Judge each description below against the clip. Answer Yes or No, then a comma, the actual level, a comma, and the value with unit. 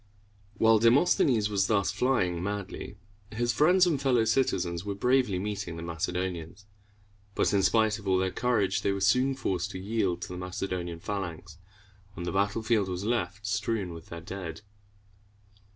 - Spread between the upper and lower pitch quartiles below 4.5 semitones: Yes, average, 3.8 semitones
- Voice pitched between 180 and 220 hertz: No, low, 100 Hz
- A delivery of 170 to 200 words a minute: No, average, 160 wpm